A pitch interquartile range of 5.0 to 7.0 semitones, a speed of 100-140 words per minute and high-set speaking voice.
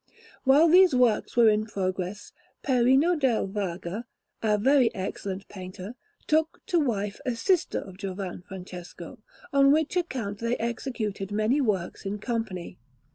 Yes: wide, 5.4 semitones; slow, 135 wpm; high, 220 Hz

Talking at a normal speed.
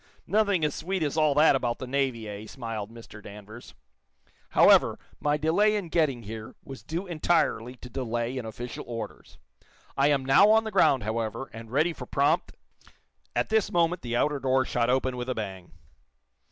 Yes: average, 180 wpm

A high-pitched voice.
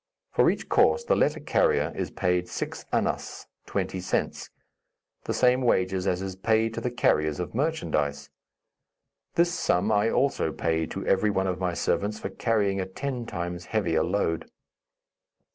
No: very low, 95 Hz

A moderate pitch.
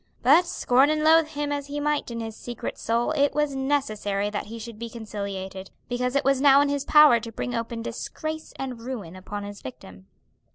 No: high, 245 Hz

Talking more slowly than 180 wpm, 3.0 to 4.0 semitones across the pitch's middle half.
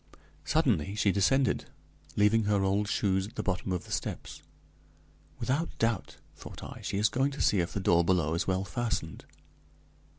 Yes: average, 170 wpm; average, 3.4 semitones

